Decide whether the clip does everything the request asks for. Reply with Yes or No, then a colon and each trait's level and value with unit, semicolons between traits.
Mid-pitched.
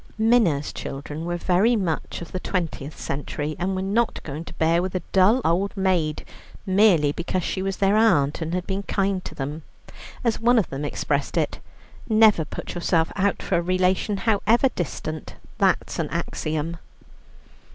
Yes: medium, 180 Hz